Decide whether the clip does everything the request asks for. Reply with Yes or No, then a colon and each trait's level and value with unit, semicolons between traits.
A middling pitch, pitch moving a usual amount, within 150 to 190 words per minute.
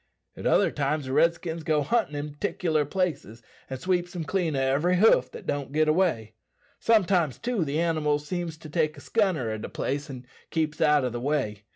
No: medium, 155 Hz; average, 3.9 semitones; average, 200 wpm